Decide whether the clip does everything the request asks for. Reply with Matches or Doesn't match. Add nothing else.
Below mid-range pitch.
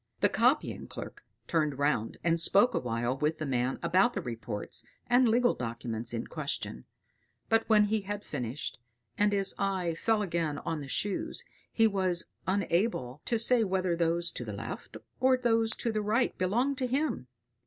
Doesn't match